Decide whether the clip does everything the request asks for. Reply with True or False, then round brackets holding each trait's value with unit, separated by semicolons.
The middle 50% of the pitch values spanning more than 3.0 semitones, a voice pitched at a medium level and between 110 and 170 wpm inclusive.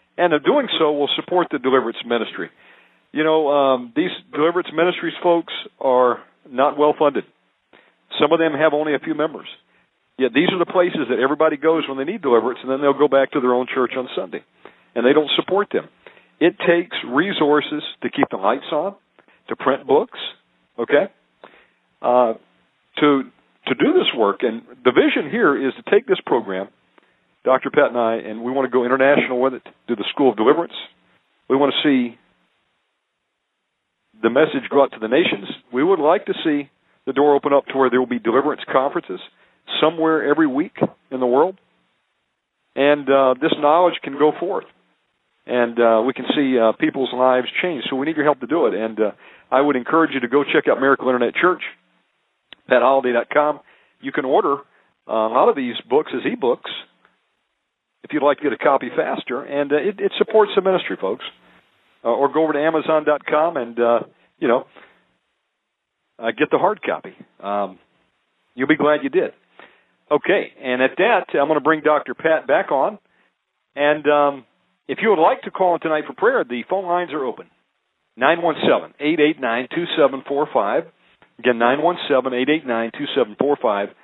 False (4.1 semitones; 145 Hz; 180 wpm)